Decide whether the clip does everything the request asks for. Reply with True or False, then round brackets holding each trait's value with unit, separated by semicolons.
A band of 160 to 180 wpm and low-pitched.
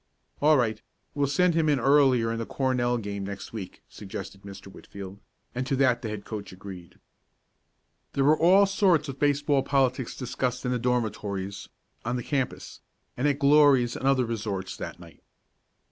True (170 wpm; 125 Hz)